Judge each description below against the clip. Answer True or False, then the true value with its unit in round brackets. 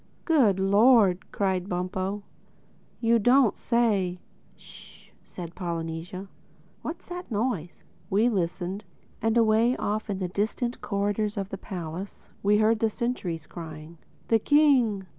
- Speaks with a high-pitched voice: True (205 Hz)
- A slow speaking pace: True (125 wpm)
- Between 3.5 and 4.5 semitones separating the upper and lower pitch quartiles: True (3.9 semitones)